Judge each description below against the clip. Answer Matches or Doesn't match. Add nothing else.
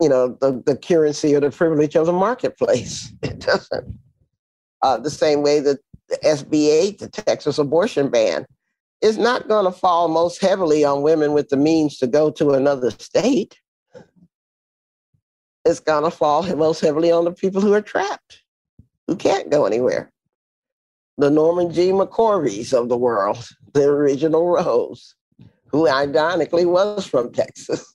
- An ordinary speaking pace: Matches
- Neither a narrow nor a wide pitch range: Matches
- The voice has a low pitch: Doesn't match